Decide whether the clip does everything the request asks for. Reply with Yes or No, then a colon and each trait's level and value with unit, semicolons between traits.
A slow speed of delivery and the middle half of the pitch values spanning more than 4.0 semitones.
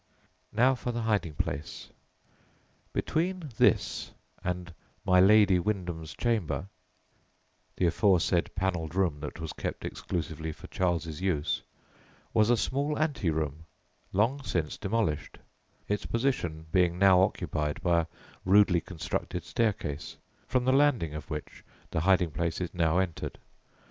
Yes: slow, 130 wpm; average, 4.8 semitones